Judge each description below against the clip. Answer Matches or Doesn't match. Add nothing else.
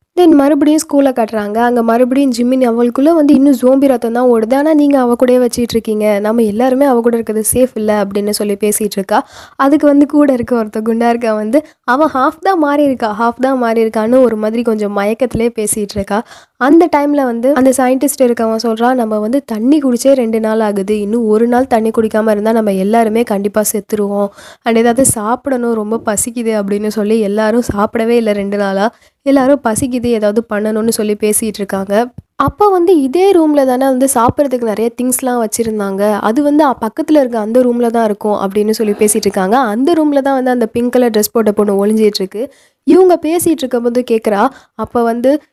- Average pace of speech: Doesn't match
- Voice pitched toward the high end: Matches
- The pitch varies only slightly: Doesn't match